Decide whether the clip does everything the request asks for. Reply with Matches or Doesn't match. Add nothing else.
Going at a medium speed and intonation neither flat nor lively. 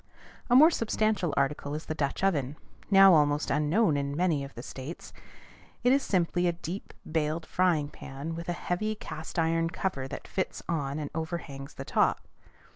Matches